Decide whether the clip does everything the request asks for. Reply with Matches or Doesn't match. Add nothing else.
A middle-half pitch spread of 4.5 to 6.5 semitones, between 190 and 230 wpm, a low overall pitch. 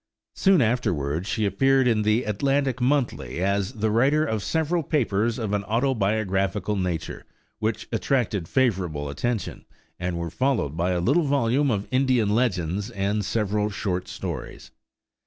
Doesn't match